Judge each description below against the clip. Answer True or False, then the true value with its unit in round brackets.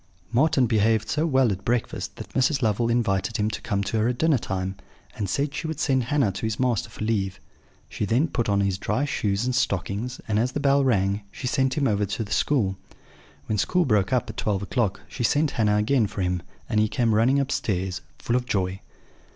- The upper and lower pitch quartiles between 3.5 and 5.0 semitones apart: True (4.5 semitones)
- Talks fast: True (215 wpm)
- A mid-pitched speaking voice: False (115 Hz)